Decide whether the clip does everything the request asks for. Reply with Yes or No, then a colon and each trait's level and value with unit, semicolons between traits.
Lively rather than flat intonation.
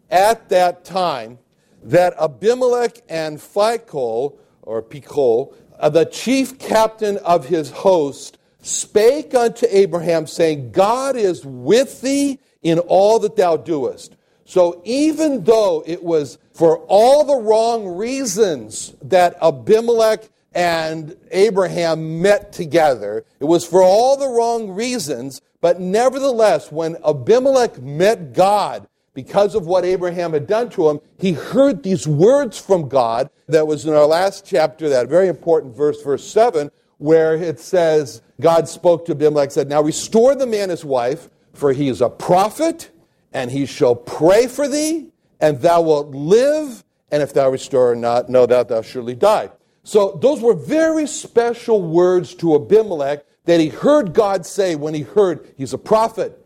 Yes: wide, 7.0 semitones